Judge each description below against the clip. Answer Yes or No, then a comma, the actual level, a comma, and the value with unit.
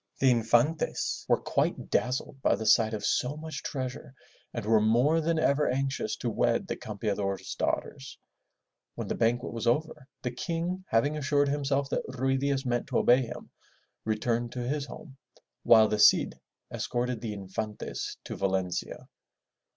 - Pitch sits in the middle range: No, low, 125 Hz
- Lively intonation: No, average, 4.2 semitones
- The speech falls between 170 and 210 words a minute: No, average, 160 wpm